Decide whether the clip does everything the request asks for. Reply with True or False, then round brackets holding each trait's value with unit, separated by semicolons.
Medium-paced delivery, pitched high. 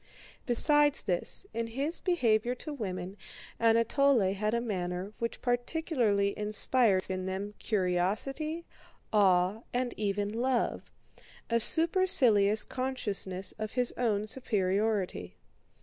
False (100 wpm; 220 Hz)